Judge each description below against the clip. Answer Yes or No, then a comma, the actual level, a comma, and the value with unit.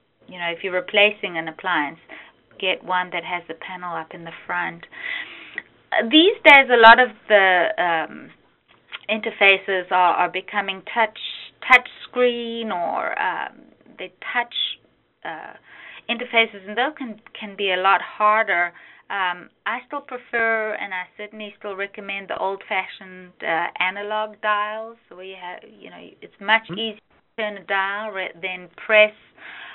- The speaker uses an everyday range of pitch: Yes, average, 3.6 semitones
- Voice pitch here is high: Yes, high, 205 Hz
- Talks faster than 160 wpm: No, average, 150 wpm